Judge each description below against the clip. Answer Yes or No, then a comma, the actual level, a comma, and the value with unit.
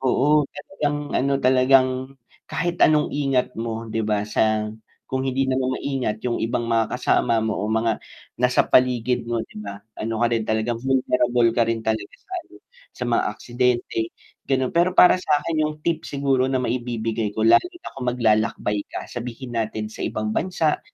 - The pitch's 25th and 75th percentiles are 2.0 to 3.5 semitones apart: Yes, average, 3.1 semitones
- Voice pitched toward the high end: No, low, 125 Hz